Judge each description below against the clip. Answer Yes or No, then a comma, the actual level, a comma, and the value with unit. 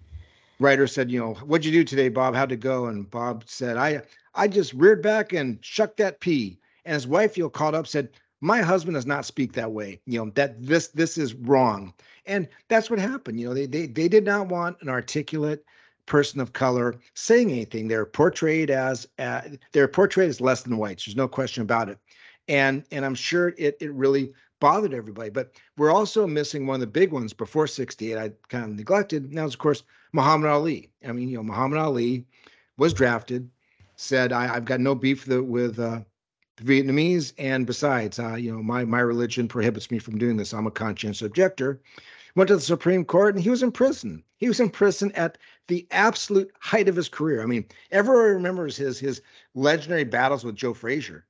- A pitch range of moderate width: No, wide, 5.7 semitones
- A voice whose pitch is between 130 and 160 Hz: Yes, low, 135 Hz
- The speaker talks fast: Yes, fast, 210 wpm